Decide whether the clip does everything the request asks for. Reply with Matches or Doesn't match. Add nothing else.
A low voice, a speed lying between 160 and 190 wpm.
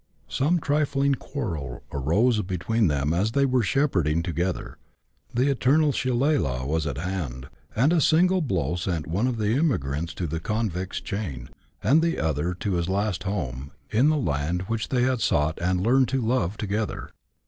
Matches